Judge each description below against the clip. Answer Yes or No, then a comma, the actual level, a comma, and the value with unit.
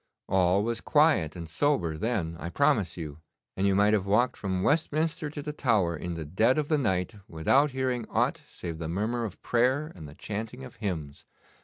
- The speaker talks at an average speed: Yes, average, 195 wpm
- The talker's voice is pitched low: Yes, low, 105 Hz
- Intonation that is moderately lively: No, wide, 7.4 semitones